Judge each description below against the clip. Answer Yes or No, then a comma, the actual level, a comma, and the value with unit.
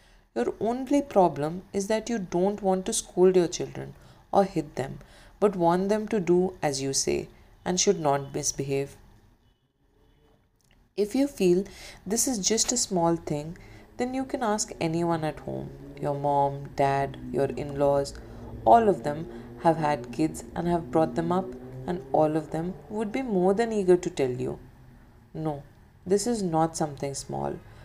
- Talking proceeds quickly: No, average, 170 wpm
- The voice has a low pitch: No, medium, 165 Hz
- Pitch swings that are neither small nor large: No, wide, 6.0 semitones